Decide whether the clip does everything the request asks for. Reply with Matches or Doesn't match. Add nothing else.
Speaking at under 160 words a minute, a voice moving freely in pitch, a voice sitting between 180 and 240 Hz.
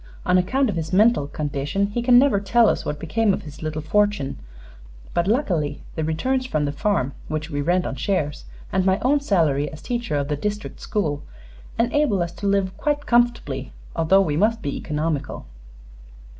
Doesn't match